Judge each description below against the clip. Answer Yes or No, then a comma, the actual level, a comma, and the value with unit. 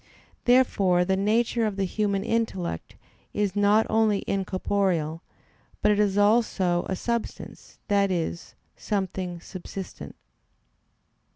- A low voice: No, high, 200 Hz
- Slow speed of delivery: Yes, slow, 110 wpm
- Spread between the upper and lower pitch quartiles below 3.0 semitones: Yes, narrow, 2.4 semitones